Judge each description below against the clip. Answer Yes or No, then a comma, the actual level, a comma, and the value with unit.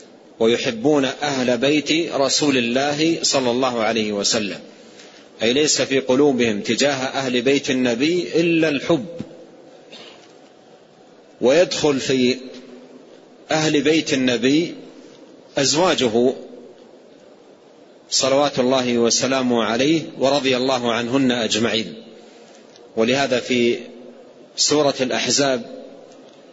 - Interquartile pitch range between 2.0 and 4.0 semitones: Yes, average, 2.8 semitones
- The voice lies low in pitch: Yes, low, 130 Hz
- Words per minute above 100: No, average, 85 wpm